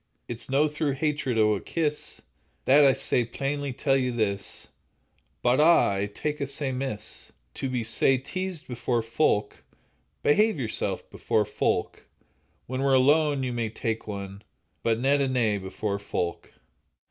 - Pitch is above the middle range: No, low, 130 Hz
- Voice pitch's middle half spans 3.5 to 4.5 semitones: Yes, average, 4.2 semitones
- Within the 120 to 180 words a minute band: Yes, average, 155 wpm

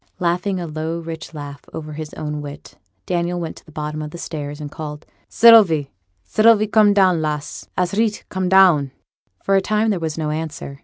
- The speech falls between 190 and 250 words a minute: Yes, average, 195 wpm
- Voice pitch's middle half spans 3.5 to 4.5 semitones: Yes, average, 4.0 semitones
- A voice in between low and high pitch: Yes, medium, 165 Hz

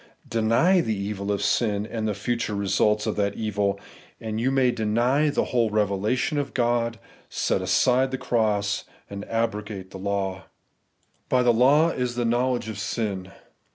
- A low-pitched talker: Yes, low, 110 Hz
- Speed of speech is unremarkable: Yes, average, 165 wpm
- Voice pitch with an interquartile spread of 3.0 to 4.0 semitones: Yes, average, 3.3 semitones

